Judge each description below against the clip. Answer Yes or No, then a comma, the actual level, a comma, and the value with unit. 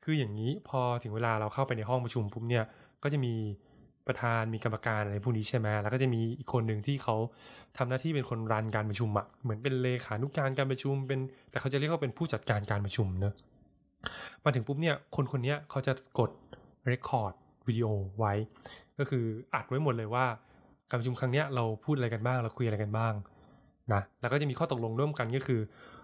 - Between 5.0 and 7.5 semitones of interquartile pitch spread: No, average, 3.3 semitones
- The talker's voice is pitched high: No, low, 125 Hz